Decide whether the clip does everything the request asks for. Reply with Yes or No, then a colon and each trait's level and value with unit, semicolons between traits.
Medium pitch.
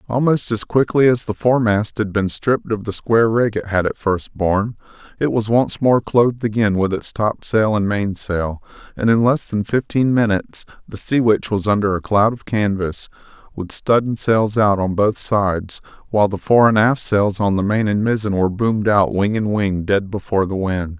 No: low, 105 Hz